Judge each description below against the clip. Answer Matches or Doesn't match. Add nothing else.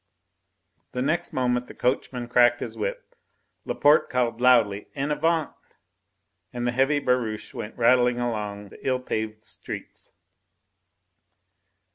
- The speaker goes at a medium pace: Doesn't match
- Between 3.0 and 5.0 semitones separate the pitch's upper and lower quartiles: Doesn't match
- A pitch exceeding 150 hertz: Doesn't match